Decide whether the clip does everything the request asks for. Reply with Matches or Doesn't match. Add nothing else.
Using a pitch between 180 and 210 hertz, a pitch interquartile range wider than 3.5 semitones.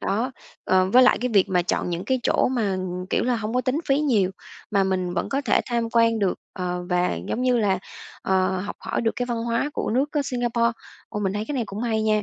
Doesn't match